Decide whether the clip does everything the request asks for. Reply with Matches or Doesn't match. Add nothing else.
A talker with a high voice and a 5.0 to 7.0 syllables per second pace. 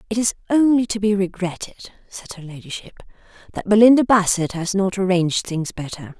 Matches